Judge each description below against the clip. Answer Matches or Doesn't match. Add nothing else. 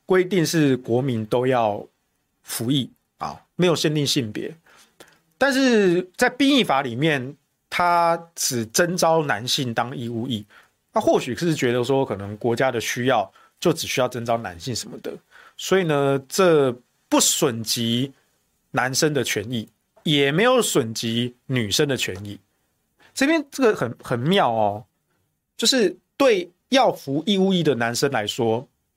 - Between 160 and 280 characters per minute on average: Matches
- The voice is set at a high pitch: Doesn't match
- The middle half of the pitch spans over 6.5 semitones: Matches